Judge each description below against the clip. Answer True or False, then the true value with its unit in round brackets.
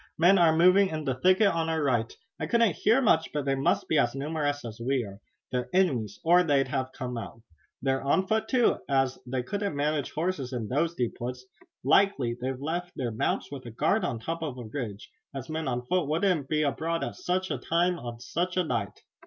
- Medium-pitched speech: True (145 Hz)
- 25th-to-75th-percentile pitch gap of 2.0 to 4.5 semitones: False (5.4 semitones)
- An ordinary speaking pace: False (220 wpm)